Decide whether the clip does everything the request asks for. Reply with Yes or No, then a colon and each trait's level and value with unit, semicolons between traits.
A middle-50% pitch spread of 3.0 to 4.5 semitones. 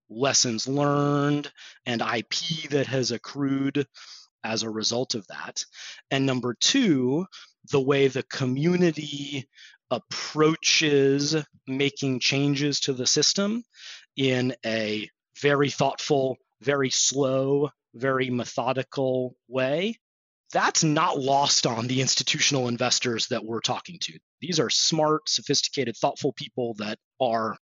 No: narrow, 2.4 semitones